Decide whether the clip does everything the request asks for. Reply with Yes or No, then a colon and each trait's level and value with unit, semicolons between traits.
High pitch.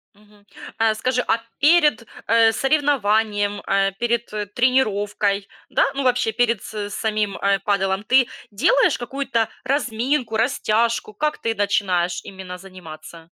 Yes: high, 220 Hz